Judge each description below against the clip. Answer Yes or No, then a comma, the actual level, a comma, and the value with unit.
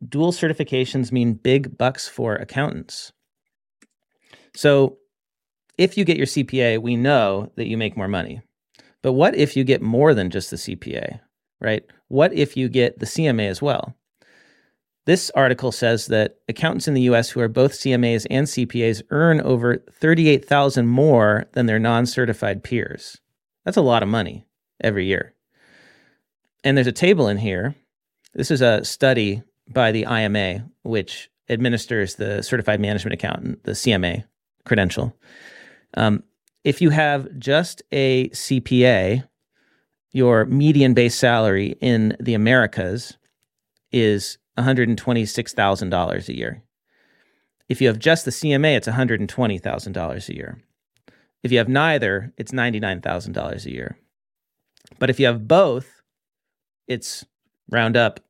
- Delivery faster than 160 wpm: No, average, 140 wpm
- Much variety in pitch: No, average, 3.6 semitones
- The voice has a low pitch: Yes, low, 125 Hz